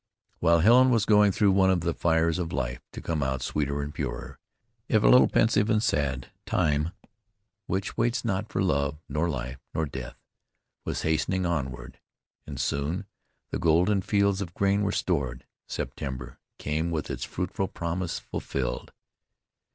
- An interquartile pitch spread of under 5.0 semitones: No, wide, 5.6 semitones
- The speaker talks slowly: No, average, 160 wpm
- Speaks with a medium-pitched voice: No, very low, 85 Hz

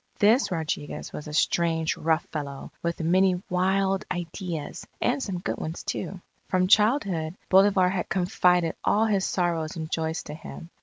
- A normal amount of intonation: Yes, average, 3.0 semitones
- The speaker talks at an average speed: Yes, average, 155 wpm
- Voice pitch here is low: No, medium, 175 Hz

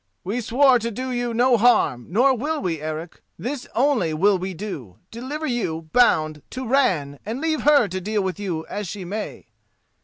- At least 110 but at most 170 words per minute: No, average, 185 wpm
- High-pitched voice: Yes, high, 215 Hz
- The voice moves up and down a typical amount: No, wide, 6.6 semitones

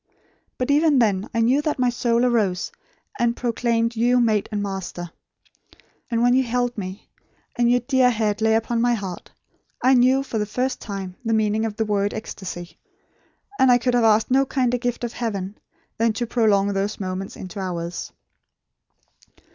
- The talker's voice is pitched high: Yes, high, 230 Hz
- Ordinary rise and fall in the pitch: Yes, average, 3.3 semitones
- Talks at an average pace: Yes, average, 175 wpm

